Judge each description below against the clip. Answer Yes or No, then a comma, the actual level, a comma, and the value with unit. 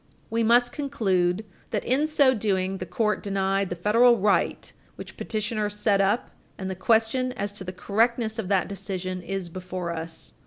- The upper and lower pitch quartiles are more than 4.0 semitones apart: No, average, 3.5 semitones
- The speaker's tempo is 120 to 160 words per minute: No, average, 170 wpm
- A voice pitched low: No, high, 200 Hz